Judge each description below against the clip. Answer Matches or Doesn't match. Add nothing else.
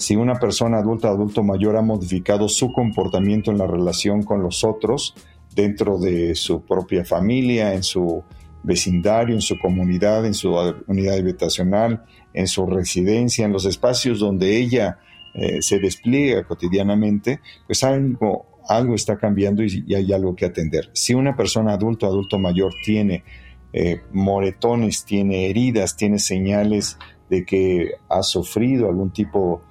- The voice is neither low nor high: Doesn't match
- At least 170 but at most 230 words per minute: Doesn't match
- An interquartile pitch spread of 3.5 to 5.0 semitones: Doesn't match